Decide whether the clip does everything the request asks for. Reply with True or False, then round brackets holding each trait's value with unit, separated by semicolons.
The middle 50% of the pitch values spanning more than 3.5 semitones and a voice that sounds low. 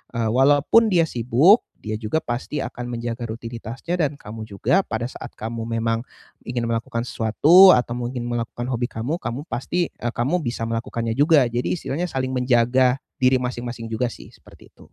False (2.8 semitones; 120 Hz)